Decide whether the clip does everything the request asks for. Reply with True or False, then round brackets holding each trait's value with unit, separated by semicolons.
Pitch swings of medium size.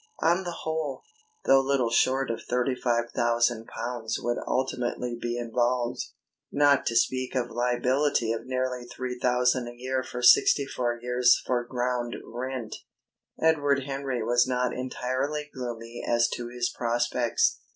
False (1.5 semitones)